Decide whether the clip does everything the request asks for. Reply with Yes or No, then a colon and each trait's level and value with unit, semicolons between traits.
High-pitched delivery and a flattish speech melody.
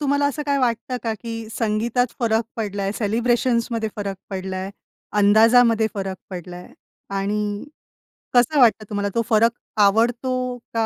No: high, 225 Hz; average, 3.1 semitones